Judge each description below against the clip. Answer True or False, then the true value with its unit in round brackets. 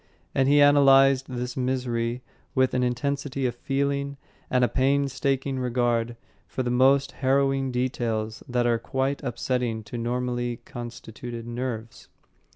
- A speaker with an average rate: False (130 wpm)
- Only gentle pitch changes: True (2.1 semitones)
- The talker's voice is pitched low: True (125 Hz)